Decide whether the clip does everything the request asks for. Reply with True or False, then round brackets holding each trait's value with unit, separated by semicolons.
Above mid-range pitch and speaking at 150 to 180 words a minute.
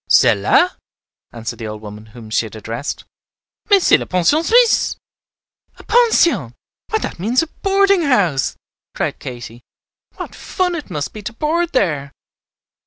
True (205 Hz; 155 wpm)